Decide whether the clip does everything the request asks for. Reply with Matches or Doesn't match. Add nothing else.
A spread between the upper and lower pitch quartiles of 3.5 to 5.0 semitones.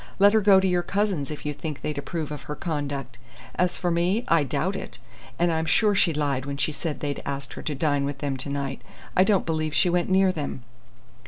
Matches